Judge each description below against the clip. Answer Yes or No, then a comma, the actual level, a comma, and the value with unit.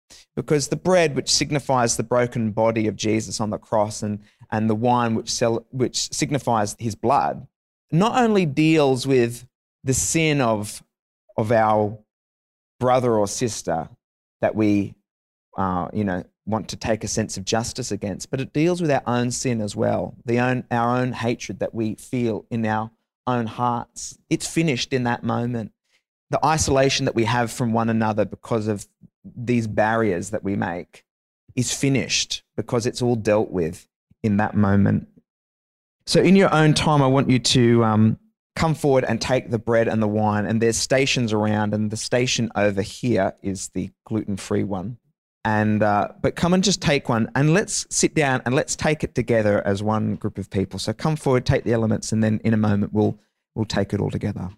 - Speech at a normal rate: Yes, average, 190 wpm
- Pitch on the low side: Yes, low, 115 Hz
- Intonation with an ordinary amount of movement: Yes, average, 3.3 semitones